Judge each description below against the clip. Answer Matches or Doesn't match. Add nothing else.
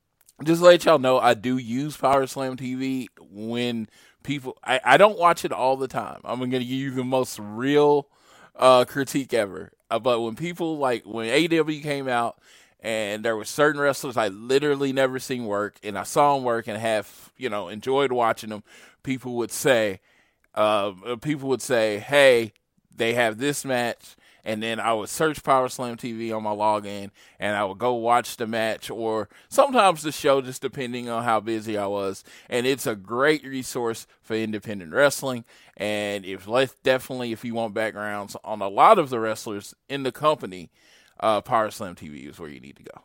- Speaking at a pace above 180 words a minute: Matches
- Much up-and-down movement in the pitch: Doesn't match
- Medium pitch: Doesn't match